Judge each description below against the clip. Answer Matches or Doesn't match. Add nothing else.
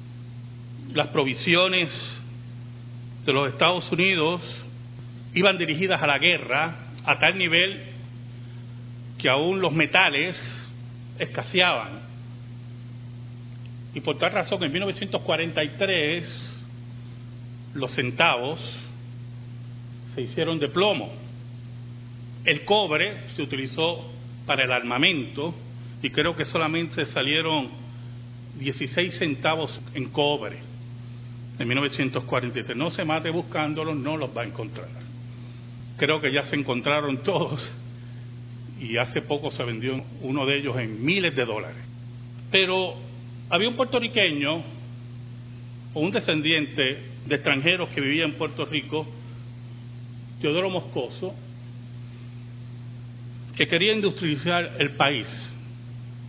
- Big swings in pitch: Doesn't match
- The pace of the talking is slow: Matches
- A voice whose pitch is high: Doesn't match